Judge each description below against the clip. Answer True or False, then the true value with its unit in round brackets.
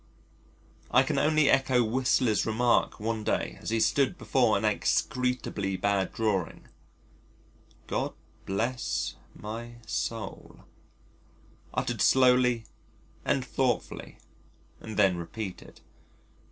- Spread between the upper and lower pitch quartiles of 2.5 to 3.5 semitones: True (3.2 semitones)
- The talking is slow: True (100 wpm)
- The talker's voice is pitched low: True (115 Hz)